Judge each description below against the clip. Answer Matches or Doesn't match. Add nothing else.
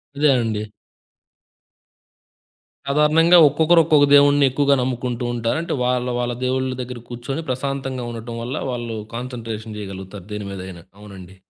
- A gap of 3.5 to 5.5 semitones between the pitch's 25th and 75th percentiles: Matches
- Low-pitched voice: Matches